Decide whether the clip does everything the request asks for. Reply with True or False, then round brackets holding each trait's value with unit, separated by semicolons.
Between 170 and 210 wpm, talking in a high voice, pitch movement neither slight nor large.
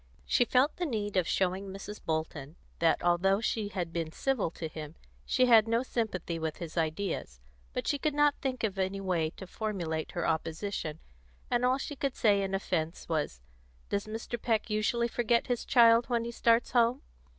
False (185 wpm; 200 Hz; 5.9 semitones)